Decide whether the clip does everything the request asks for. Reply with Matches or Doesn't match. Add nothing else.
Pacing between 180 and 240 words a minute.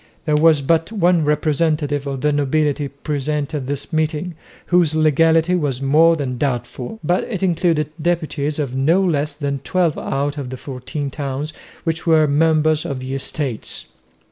Doesn't match